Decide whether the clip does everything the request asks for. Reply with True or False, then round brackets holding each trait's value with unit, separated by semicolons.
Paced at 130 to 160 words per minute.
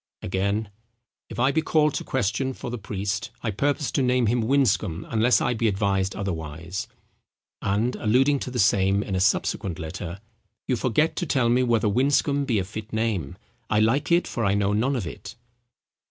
False (185 wpm)